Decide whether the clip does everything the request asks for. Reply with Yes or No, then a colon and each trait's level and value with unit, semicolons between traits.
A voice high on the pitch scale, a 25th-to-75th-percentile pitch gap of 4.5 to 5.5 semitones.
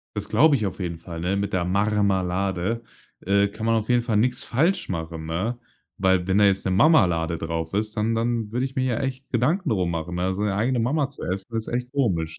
No: low, 105 Hz; average, 4.8 semitones